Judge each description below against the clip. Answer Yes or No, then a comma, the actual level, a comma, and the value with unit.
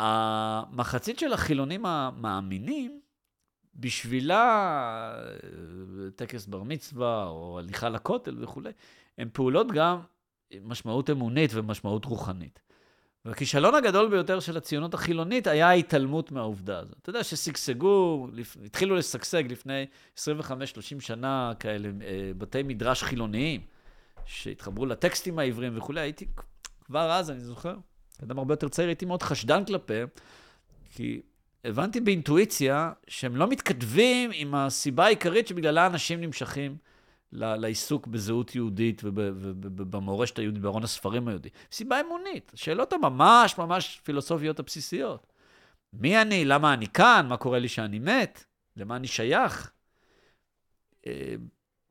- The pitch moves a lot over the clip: Yes, wide, 7.2 semitones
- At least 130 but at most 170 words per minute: No, average, 115 wpm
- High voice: No, low, 135 Hz